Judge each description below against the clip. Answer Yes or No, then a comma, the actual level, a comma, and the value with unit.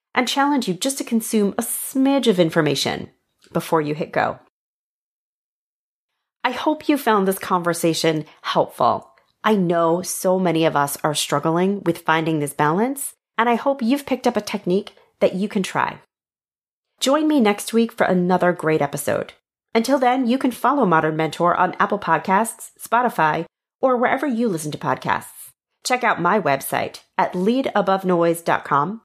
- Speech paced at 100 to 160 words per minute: Yes, average, 155 wpm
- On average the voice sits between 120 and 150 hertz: No, high, 195 Hz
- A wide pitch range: Yes, wide, 6.5 semitones